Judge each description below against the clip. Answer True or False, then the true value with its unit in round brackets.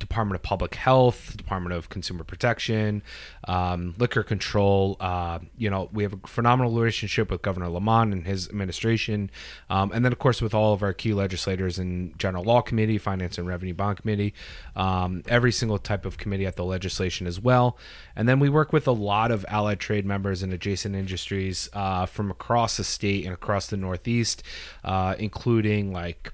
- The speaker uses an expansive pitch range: False (3.2 semitones)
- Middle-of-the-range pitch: False (100 Hz)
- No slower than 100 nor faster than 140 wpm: False (190 wpm)